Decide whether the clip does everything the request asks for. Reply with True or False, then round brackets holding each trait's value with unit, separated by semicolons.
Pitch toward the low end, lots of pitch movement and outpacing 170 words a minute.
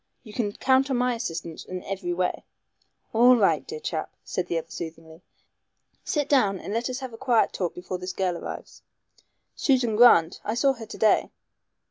False (215 Hz; 5.8 semitones; 190 wpm)